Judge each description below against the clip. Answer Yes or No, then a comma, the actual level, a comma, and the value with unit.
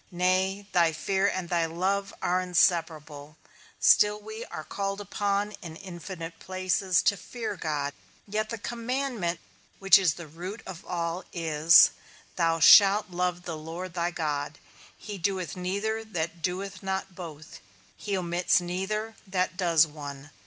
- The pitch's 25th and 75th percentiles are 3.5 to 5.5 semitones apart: No, average, 3.0 semitones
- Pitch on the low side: No, medium, 180 Hz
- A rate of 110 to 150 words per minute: Yes, average, 145 wpm